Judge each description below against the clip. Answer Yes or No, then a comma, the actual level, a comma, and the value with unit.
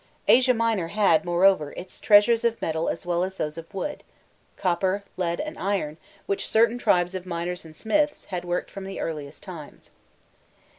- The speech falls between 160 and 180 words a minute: Yes, average, 170 wpm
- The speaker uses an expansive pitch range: No, average, 3.9 semitones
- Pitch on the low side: No, medium, 185 Hz